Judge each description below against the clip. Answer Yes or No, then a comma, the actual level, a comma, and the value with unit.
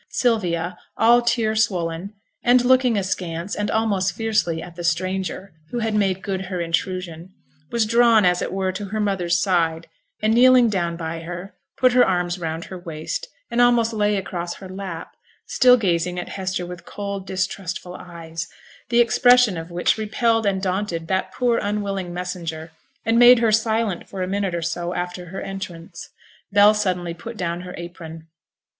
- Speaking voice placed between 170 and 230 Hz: Yes, high, 190 Hz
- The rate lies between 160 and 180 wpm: Yes, average, 170 wpm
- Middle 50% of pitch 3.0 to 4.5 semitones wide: Yes, average, 3.8 semitones